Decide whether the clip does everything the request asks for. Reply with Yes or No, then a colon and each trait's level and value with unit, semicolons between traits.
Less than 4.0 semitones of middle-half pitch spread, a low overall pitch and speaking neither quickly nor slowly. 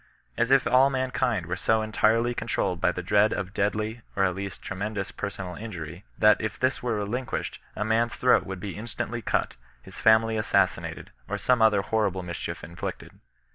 Yes: average, 3.0 semitones; low, 110 Hz; average, 185 wpm